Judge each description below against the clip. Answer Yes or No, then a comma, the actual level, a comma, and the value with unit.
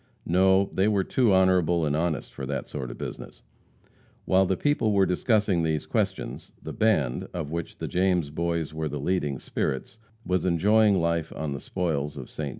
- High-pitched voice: No, very low, 85 Hz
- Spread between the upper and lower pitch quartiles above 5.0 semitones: No, average, 3.8 semitones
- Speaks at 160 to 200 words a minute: Yes, average, 180 wpm